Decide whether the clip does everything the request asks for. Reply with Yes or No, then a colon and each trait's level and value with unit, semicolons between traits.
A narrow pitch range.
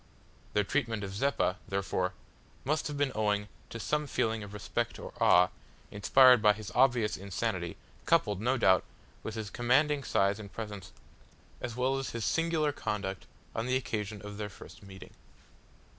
No: average, 4.2 semitones